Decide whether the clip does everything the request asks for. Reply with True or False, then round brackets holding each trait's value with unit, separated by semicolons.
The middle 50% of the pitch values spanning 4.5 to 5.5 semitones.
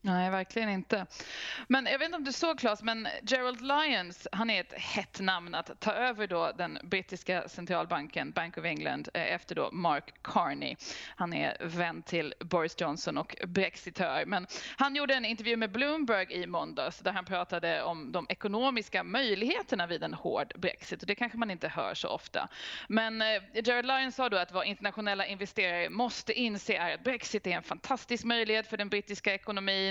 True (4.8 semitones)